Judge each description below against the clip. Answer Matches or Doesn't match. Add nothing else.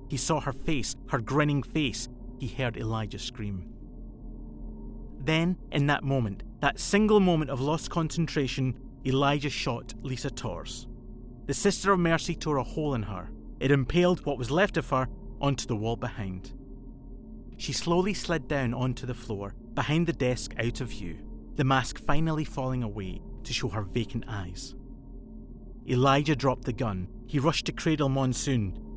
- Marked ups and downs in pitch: Doesn't match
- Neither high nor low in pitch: Doesn't match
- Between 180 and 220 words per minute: Doesn't match